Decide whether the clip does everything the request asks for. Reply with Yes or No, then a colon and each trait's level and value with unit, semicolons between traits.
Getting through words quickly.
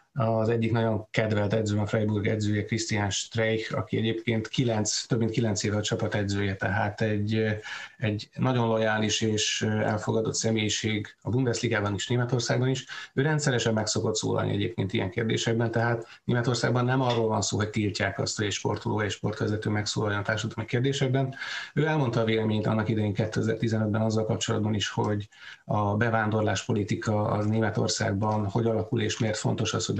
Yes: fast, 160 wpm